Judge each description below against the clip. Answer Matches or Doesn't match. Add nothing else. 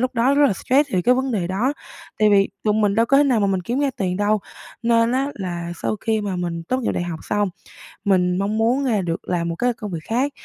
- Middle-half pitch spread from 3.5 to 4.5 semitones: Doesn't match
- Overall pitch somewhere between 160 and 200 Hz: Doesn't match